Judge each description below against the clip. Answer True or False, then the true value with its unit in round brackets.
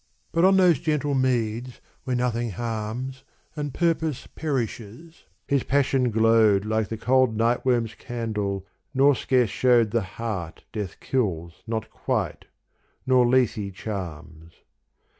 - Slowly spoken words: True (120 wpm)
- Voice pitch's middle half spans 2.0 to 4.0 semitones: True (3.5 semitones)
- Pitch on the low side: True (120 Hz)